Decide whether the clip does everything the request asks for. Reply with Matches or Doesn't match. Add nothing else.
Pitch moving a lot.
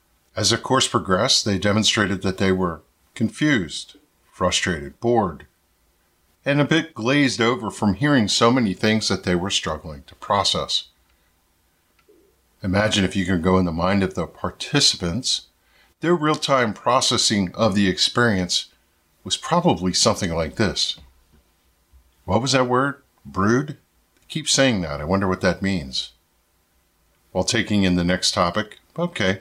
Matches